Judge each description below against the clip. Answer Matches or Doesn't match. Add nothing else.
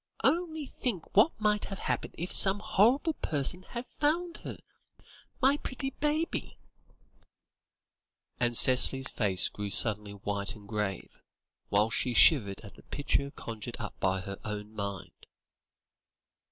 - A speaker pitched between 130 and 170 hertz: Matches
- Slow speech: Matches